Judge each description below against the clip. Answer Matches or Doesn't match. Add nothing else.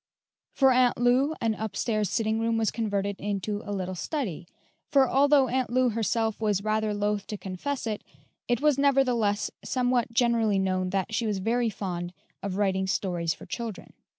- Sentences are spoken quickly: Doesn't match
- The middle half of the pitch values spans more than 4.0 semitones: Doesn't match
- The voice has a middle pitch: Doesn't match